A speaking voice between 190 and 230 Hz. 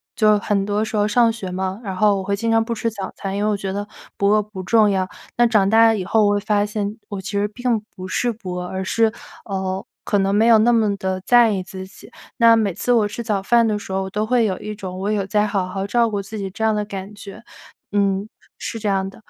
Yes: high, 205 Hz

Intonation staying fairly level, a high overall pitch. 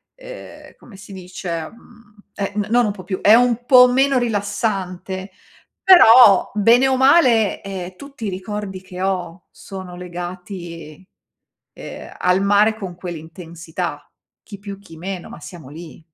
No: average, 3.9 semitones; high, 195 Hz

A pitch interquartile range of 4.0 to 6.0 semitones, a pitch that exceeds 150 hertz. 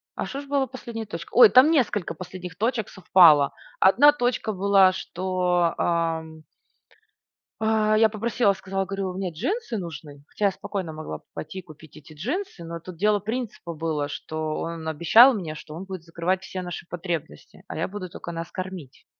Yes: average, 4.5 semitones; medium, 185 Hz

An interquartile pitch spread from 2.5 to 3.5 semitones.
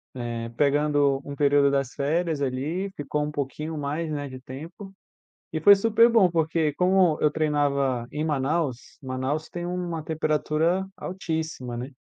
Yes: average, 3.2 semitones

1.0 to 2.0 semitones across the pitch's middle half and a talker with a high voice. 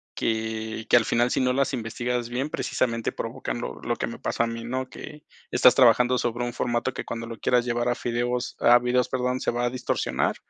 No: narrow, 1.4 semitones; low, 120 Hz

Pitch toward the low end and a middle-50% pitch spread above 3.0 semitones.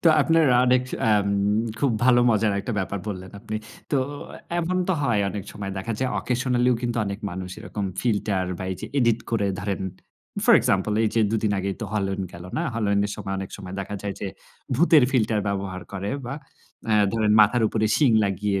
Yes: low, 105 Hz; average, 3.7 semitones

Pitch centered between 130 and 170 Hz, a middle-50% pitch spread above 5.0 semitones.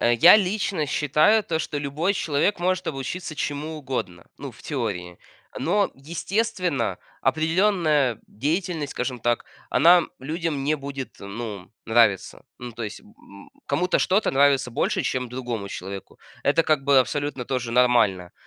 Yes: medium, 140 Hz; wide, 5.5 semitones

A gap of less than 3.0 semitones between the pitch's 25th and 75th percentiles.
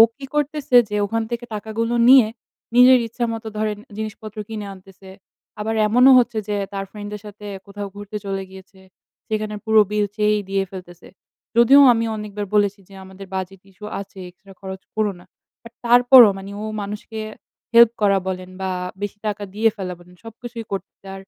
Yes: narrow, 2.6 semitones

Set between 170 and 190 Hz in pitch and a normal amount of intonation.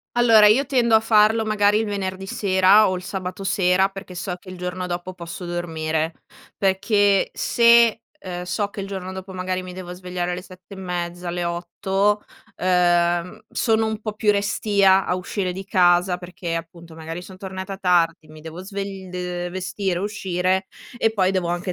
No: medium, 185 Hz; narrow, 2.2 semitones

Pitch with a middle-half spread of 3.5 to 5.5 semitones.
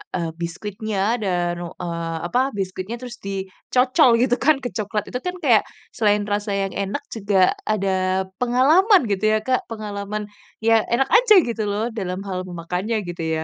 Yes: average, 4.3 semitones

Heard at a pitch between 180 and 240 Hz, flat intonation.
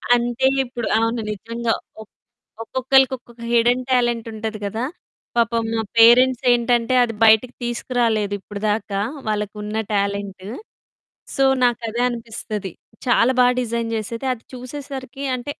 Yes: high, 235 Hz; narrow, 2.1 semitones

